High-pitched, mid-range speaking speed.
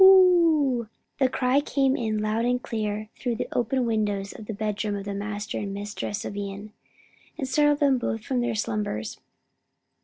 Yes: high, 220 Hz; average, 175 wpm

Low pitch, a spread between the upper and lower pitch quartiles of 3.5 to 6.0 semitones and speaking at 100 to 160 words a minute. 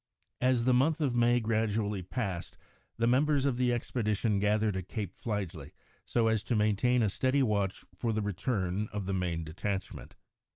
No: low, 110 Hz; average, 3.8 semitones; average, 175 wpm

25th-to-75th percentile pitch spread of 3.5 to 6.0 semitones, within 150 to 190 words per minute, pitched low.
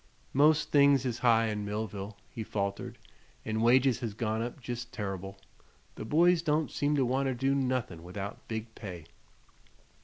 Yes: average, 4.4 semitones; average, 155 wpm; low, 115 Hz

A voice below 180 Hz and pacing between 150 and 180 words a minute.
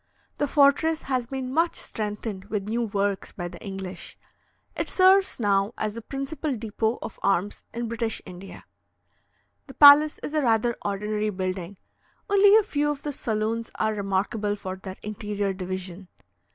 No: high, 215 Hz; average, 155 wpm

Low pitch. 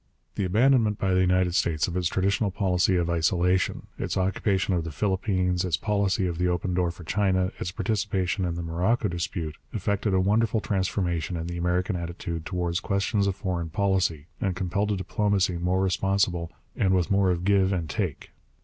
Yes: very low, 95 Hz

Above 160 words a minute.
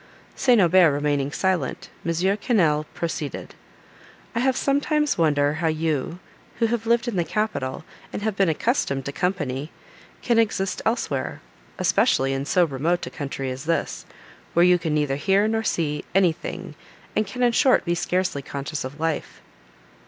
No: average, 155 wpm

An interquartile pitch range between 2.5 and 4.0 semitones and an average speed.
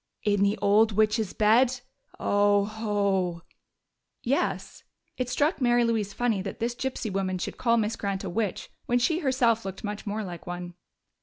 Yes: average, 3.2 semitones; average, 165 wpm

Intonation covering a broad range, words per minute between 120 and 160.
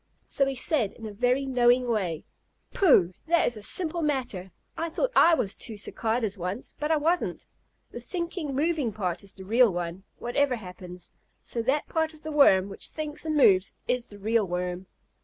No: wide, 7.5 semitones; average, 190 wpm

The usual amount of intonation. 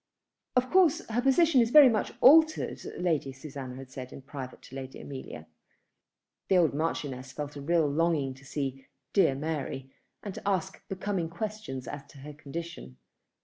No: wide, 6.8 semitones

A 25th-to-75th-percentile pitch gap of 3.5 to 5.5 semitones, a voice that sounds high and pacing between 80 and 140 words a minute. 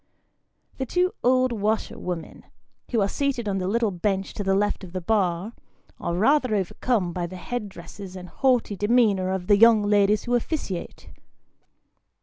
No: average, 4.1 semitones; high, 205 Hz; average, 155 wpm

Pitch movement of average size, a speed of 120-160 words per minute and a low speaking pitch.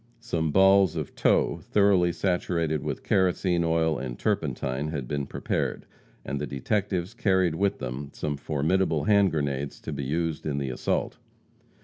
Yes: average, 4.8 semitones; average, 150 wpm; very low, 80 Hz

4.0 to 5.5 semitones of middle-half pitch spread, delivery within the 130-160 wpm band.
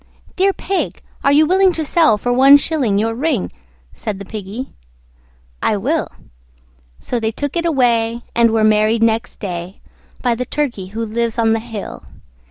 No: average, 4.6 semitones; average, 170 wpm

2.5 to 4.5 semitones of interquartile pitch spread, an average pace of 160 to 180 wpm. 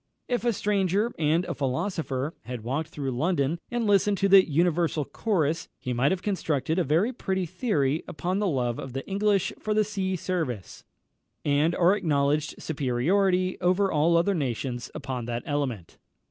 No: wide, 5.6 semitones; average, 165 wpm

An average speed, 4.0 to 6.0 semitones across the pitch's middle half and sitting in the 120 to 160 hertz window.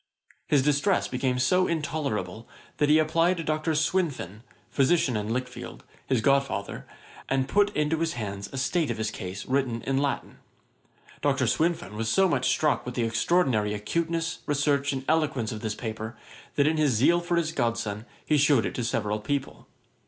Yes: average, 175 wpm; wide, 5.5 semitones; low, 135 Hz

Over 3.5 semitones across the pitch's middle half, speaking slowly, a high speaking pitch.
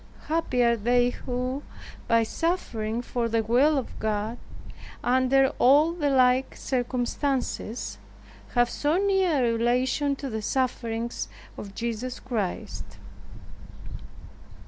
No: average, 2.9 semitones; slow, 105 wpm; very high, 250 Hz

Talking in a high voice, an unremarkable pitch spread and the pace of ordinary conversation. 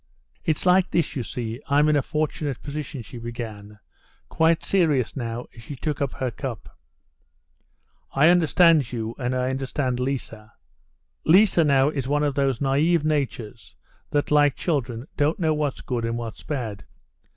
No: low, 135 Hz; average, 4.1 semitones; average, 160 wpm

